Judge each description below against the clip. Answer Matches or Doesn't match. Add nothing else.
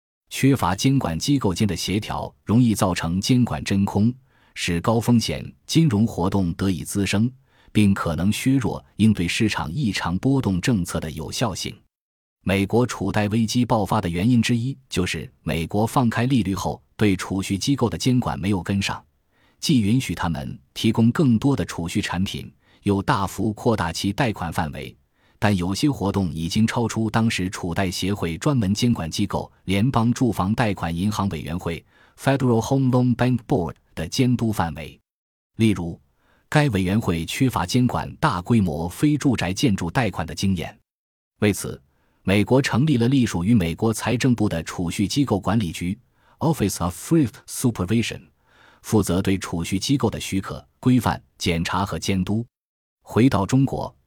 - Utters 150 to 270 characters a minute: Doesn't match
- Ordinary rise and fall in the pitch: Matches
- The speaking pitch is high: Doesn't match